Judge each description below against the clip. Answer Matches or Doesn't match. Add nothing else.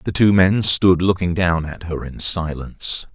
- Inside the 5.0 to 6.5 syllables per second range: Doesn't match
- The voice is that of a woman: Doesn't match